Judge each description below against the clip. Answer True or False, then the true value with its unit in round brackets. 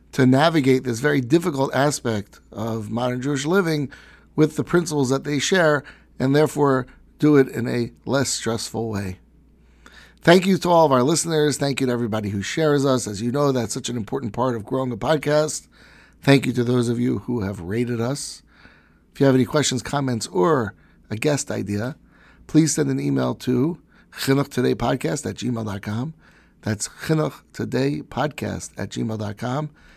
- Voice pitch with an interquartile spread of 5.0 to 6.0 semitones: False (4.0 semitones)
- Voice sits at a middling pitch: False (130 Hz)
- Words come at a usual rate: True (165 wpm)